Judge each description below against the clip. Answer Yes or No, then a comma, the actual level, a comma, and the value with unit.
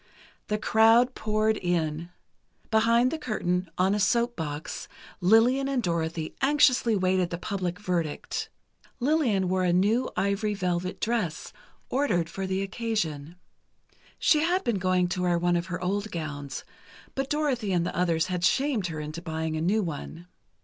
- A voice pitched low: No, high, 190 Hz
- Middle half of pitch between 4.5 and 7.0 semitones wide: Yes, average, 4.8 semitones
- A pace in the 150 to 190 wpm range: Yes, average, 155 wpm